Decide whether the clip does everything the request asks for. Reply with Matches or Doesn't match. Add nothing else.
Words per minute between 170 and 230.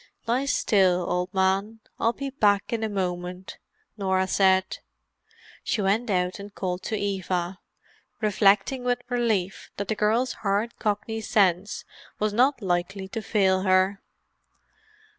Doesn't match